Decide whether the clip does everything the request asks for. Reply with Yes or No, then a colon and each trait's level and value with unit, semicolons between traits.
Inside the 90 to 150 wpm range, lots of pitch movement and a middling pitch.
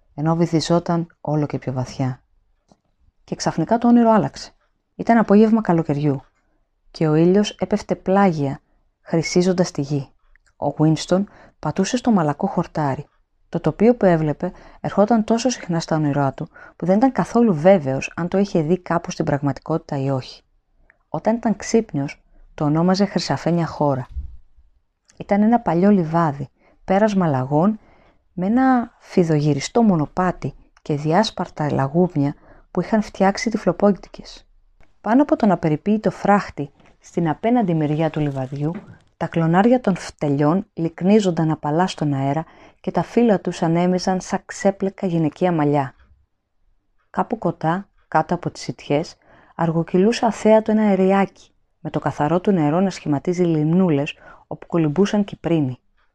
No: average, 135 wpm; average, 4.9 semitones; medium, 170 Hz